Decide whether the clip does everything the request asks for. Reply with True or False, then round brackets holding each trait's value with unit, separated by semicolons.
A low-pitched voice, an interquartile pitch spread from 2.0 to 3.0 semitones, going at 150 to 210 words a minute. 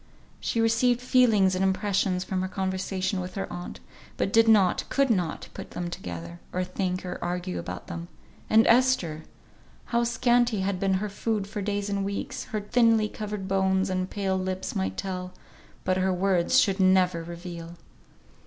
False (190 Hz; 2.6 semitones; 170 wpm)